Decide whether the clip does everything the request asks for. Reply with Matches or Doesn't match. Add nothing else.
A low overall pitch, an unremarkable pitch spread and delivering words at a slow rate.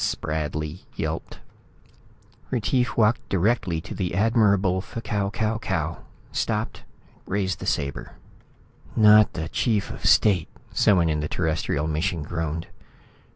Matches